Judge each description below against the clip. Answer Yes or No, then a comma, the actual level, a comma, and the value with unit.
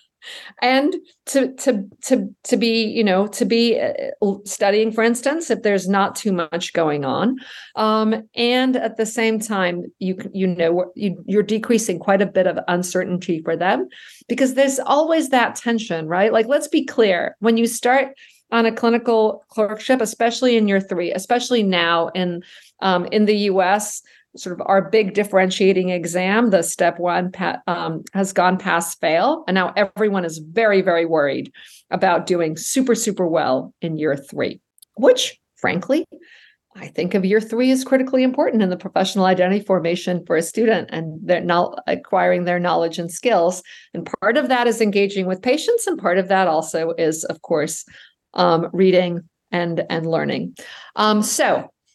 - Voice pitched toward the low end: No, high, 205 Hz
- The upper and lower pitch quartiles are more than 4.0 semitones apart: Yes, average, 4.6 semitones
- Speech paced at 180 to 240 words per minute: No, average, 165 wpm